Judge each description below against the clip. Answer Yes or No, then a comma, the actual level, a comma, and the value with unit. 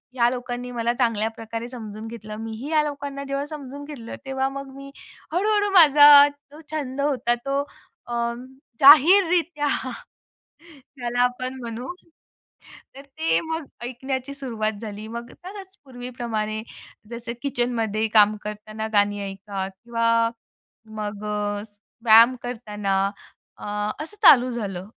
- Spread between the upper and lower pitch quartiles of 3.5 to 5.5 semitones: Yes, average, 4.2 semitones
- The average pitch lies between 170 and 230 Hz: No, high, 245 Hz